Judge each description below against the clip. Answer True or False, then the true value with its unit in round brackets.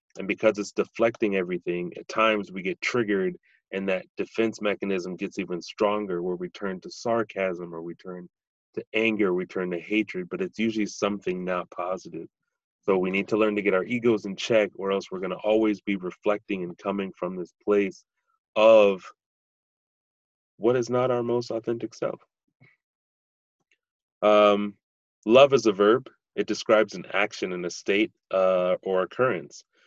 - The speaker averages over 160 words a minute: True (170 wpm)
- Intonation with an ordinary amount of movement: True (3.4 semitones)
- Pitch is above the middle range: False (100 Hz)